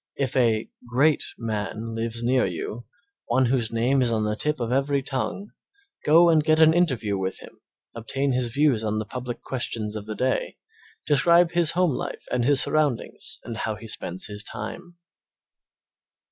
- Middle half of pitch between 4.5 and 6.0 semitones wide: Yes, average, 4.8 semitones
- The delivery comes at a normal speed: Yes, average, 175 wpm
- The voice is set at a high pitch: No, low, 125 Hz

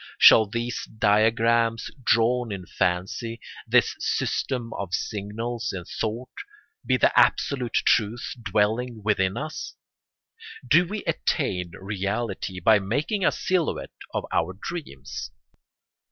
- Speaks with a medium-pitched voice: No, low, 110 Hz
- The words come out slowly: Yes, slow, 110 wpm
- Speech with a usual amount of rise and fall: Yes, average, 3.4 semitones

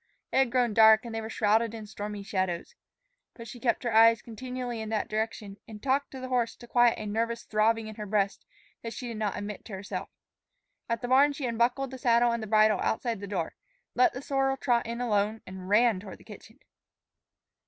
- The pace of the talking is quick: Yes, fast, 215 wpm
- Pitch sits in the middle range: No, high, 225 Hz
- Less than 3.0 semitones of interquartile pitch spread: Yes, narrow, 2.4 semitones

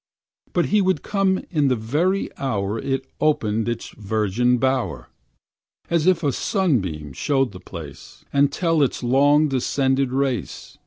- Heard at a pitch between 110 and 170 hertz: Yes, low, 135 Hz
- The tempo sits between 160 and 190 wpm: No, average, 150 wpm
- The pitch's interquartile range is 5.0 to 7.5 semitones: Yes, wide, 5.4 semitones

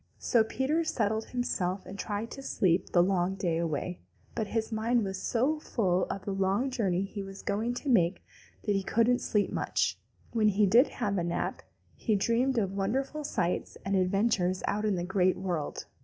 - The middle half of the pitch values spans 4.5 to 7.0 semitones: No, average, 3.8 semitones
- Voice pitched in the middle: No, high, 200 Hz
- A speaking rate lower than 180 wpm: No, average, 190 wpm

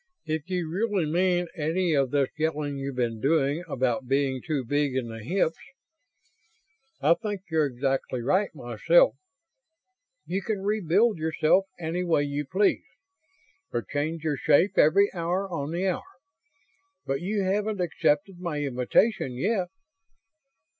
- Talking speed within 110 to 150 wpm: Yes, average, 140 wpm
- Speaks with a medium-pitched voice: Yes, medium, 160 Hz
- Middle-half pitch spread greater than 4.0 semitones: Yes, average, 5.0 semitones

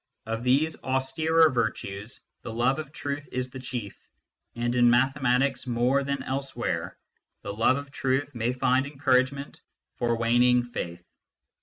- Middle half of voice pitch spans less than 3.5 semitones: Yes, narrow, 2.4 semitones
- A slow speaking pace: No, average, 150 wpm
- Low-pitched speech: Yes, low, 130 Hz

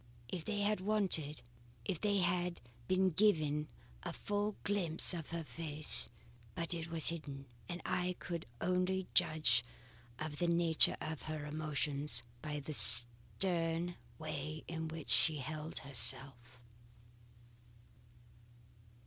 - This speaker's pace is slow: Yes, slow, 125 wpm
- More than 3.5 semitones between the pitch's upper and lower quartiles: No, average, 3.1 semitones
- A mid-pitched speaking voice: Yes, medium, 160 Hz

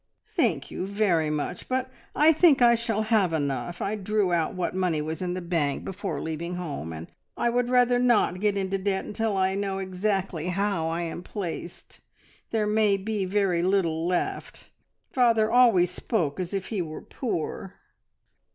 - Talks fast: No, average, 170 wpm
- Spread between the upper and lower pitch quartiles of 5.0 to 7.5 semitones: No, average, 3.9 semitones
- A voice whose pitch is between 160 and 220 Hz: Yes, high, 190 Hz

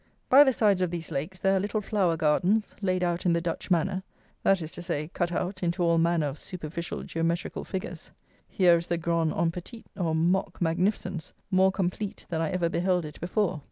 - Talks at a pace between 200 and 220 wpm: Yes, fast, 205 wpm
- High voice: No, medium, 175 Hz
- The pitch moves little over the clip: Yes, narrow, 2.3 semitones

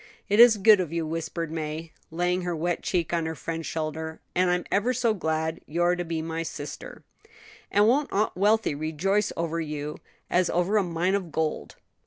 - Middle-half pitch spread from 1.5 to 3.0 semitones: No, average, 3.4 semitones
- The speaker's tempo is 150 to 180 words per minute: No, average, 190 wpm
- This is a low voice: No, medium, 170 Hz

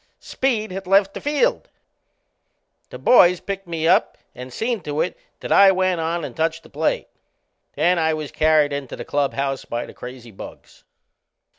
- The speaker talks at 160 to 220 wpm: Yes, average, 170 wpm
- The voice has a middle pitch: Yes, medium, 165 Hz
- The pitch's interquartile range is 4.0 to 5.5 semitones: Yes, average, 5.1 semitones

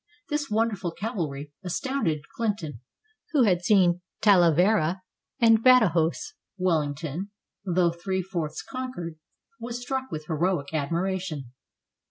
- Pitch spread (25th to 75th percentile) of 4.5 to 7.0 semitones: Yes, wide, 5.5 semitones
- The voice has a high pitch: No, medium, 180 Hz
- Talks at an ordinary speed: No, slow, 105 wpm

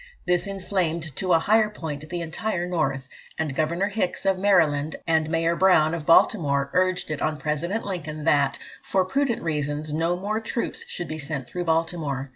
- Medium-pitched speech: Yes, medium, 165 Hz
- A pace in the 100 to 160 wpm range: No, average, 175 wpm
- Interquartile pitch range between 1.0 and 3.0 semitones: No, average, 3.4 semitones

